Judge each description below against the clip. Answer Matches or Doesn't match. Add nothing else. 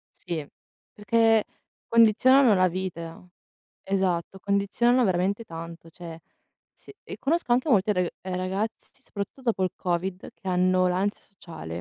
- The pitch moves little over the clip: Doesn't match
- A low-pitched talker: Doesn't match